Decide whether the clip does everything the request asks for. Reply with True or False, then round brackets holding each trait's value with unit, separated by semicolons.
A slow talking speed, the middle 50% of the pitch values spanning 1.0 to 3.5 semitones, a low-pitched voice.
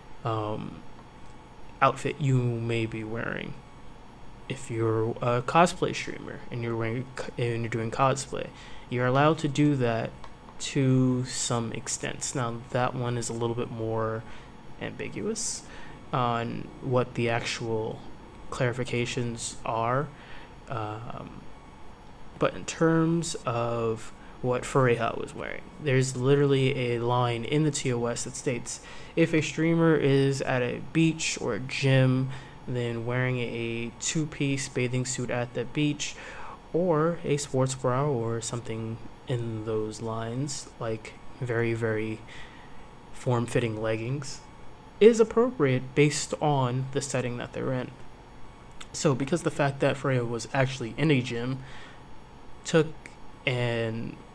True (125 wpm; 3.2 semitones; 125 Hz)